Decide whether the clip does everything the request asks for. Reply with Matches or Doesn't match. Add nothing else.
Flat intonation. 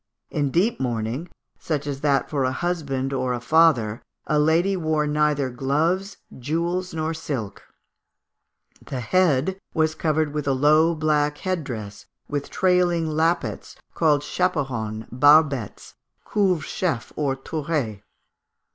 Doesn't match